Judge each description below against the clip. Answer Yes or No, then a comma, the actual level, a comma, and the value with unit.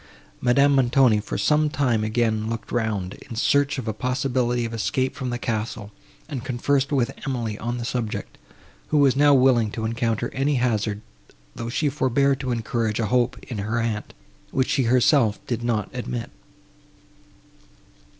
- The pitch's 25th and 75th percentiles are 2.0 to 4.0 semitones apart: Yes, average, 3.1 semitones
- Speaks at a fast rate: No, average, 160 wpm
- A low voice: Yes, low, 120 Hz